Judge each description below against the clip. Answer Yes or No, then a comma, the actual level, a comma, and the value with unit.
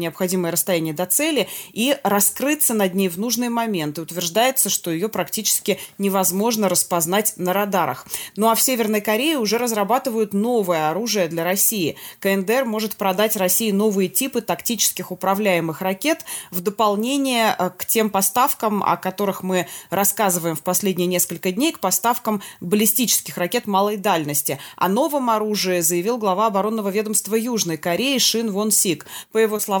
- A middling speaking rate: Yes, average, 150 wpm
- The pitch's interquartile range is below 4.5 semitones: Yes, average, 3.7 semitones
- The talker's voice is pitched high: Yes, high, 200 Hz